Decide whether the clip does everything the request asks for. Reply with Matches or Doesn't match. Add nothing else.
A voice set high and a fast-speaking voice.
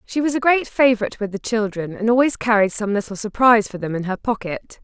Matches